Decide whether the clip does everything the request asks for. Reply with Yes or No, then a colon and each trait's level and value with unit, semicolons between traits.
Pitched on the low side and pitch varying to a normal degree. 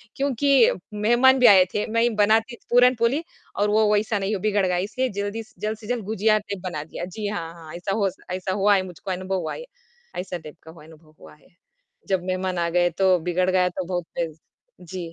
No: high, 195 Hz; average, 3.4 semitones